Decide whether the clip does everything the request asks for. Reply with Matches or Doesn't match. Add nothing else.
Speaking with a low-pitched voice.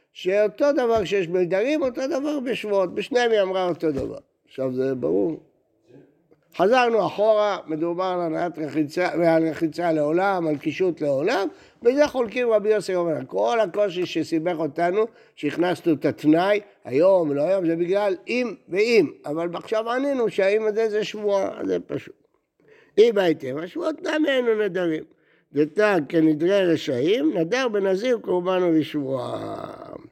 Doesn't match